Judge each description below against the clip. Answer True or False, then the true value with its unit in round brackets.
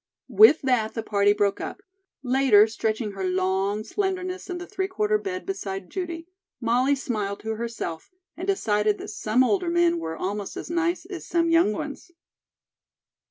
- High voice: True (250 Hz)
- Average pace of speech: True (160 wpm)